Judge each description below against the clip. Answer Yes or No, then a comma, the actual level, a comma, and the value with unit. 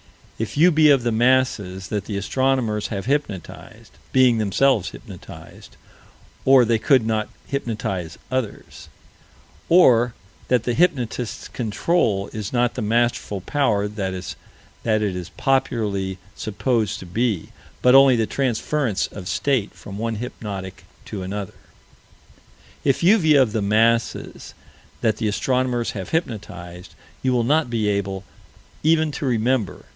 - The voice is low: Yes, low, 115 Hz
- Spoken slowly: Yes, slow, 130 wpm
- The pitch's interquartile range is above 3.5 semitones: Yes, average, 4.3 semitones